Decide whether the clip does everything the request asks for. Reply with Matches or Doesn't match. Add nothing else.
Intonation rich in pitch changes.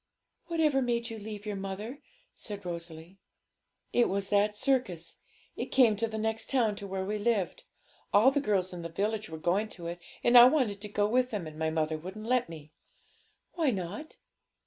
Doesn't match